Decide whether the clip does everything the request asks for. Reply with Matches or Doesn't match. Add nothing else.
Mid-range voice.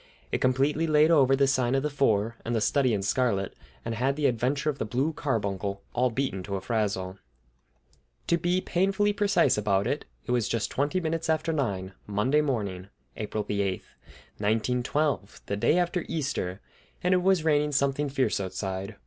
Doesn't match